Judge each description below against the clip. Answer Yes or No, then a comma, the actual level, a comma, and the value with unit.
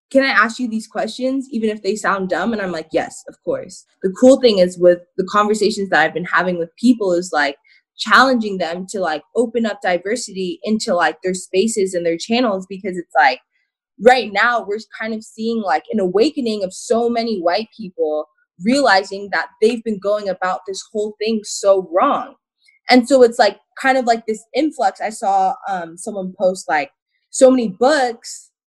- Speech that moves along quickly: No, average, 190 wpm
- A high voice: Yes, high, 215 Hz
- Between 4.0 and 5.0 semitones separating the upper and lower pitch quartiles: Yes, average, 4.7 semitones